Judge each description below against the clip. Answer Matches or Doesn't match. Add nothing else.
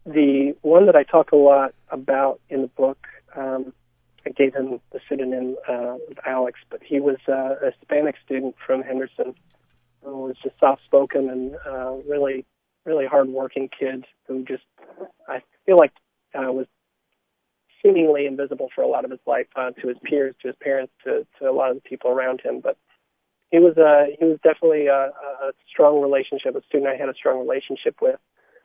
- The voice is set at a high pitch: Doesn't match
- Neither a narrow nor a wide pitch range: Doesn't match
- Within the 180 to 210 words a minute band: Matches